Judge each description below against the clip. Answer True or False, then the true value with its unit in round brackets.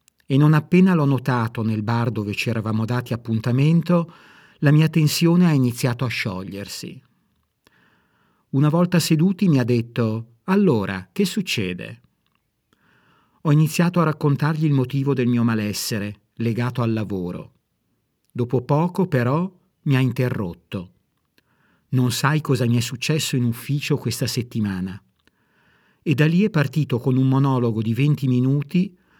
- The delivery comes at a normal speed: True (140 wpm)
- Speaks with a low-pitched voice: True (130 Hz)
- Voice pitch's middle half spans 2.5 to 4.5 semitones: False (4.9 semitones)